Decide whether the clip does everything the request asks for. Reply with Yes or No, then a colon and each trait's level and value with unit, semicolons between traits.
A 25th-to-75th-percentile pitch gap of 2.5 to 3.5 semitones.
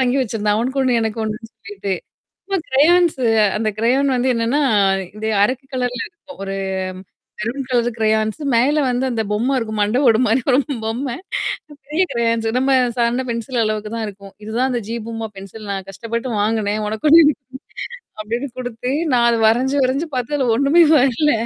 Yes: average, 3.2 semitones